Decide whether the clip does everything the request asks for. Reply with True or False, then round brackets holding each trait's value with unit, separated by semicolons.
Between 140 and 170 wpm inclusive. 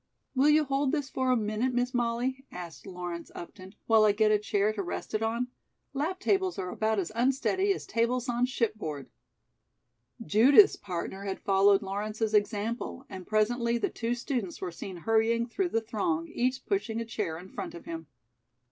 False (180 wpm)